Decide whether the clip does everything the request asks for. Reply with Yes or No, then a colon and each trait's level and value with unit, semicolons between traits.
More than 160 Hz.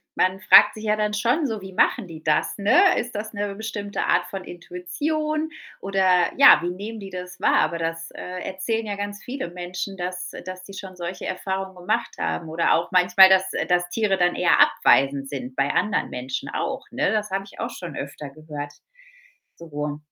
Yes: medium, 185 Hz